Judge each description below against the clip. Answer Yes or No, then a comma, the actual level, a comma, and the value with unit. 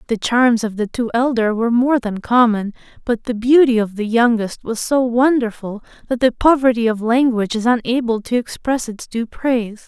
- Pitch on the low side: No, high, 235 Hz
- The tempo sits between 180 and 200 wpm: Yes, average, 190 wpm